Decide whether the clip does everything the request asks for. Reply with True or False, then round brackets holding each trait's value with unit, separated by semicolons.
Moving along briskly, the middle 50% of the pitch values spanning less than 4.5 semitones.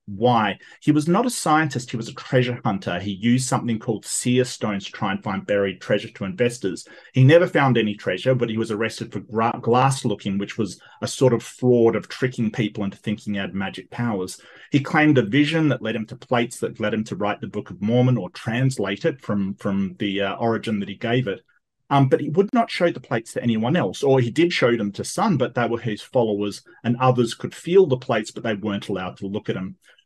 True (240 wpm; 4.1 semitones)